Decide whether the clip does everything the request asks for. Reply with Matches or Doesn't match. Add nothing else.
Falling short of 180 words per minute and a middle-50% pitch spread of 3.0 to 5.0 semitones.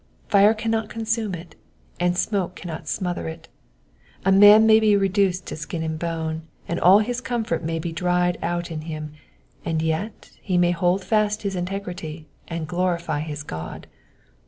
Matches